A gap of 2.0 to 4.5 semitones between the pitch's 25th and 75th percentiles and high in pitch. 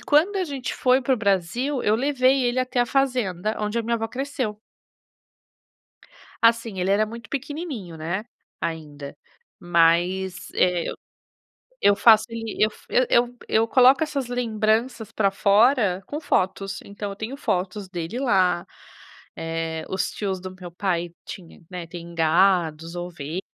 No: wide, 5.6 semitones; high, 210 Hz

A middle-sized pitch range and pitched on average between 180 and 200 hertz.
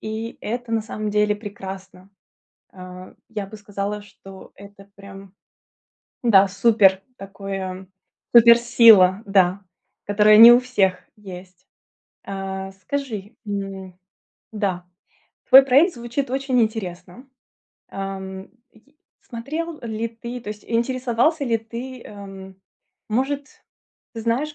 No: average, 3.5 semitones; high, 210 Hz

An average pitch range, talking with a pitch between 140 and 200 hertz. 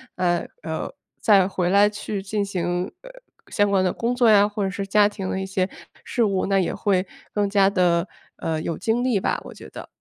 No: narrow, 2.0 semitones; high, 195 Hz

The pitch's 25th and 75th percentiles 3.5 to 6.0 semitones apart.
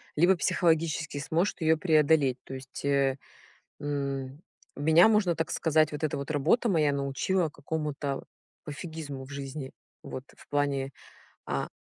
No: narrow, 2.6 semitones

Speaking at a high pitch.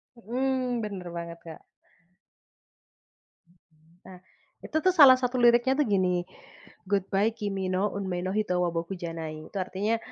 Yes: high, 195 Hz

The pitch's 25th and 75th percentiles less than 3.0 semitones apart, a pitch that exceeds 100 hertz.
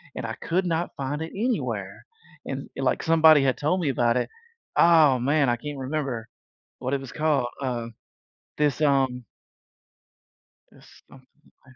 No: average, 3.4 semitones; medium, 140 Hz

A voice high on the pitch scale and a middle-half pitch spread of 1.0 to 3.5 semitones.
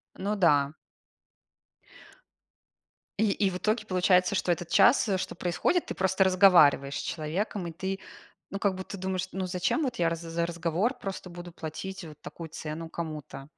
No: medium, 180 Hz; average, 2.7 semitones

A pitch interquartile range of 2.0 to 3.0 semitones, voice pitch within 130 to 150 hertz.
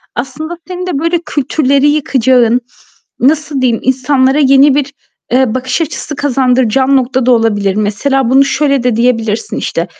No: narrow, 2.6 semitones; very high, 265 Hz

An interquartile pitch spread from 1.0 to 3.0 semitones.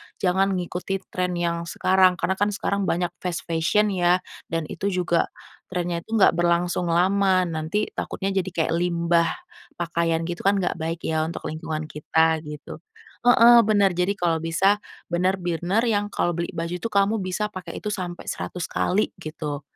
Yes: narrow, 2.5 semitones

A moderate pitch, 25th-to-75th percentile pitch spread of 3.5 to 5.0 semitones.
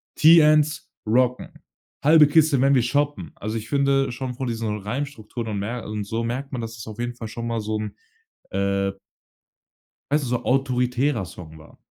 No: low, 120 Hz; average, 4.2 semitones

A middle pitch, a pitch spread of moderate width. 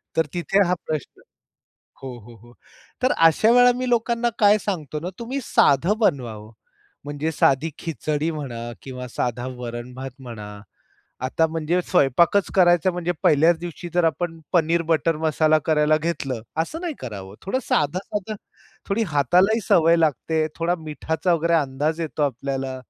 Yes: medium, 160 Hz; average, 4.7 semitones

